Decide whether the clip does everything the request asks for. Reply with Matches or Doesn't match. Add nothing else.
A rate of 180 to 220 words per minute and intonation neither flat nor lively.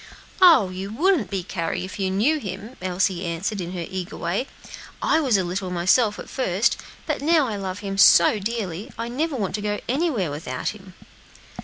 Matches